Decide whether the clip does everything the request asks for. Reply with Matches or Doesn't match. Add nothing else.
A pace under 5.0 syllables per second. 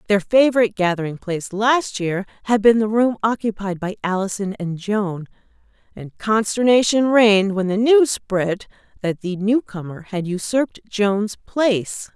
Matches